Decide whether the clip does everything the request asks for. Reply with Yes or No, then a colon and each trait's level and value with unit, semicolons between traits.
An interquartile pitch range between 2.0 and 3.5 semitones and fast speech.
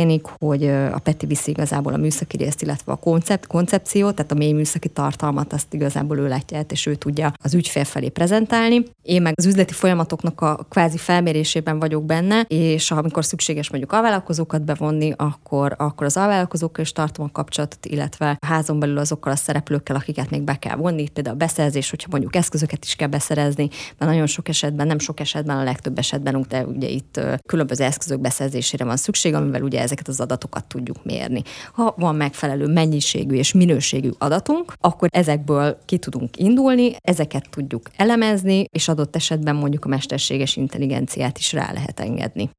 Yes: average, 2.7 semitones; fast, 175 wpm